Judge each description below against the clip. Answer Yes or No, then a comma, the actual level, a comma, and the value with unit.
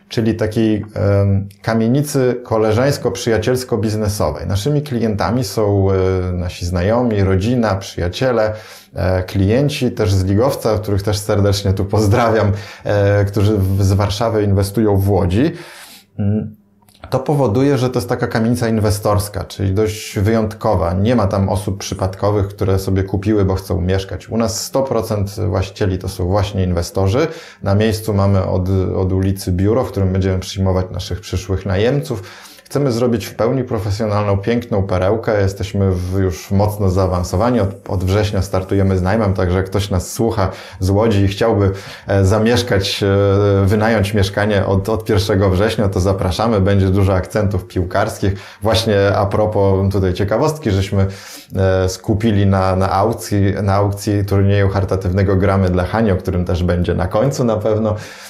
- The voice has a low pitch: Yes, low, 100 Hz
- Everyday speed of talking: Yes, average, 140 wpm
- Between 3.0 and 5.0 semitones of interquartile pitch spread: No, narrow, 2.4 semitones